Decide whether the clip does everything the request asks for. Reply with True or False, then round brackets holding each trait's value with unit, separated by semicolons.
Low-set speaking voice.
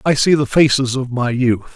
True (130 Hz)